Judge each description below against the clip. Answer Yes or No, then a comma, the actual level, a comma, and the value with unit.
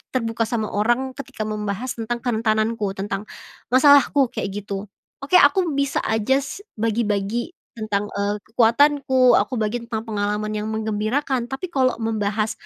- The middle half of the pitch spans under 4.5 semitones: Yes, average, 3.6 semitones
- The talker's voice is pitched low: No, high, 225 Hz